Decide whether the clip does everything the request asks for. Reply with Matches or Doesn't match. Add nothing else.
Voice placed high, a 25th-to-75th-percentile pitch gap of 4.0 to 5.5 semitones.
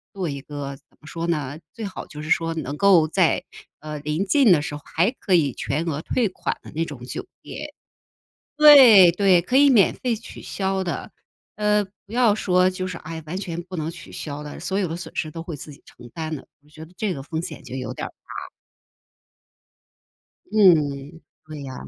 Doesn't match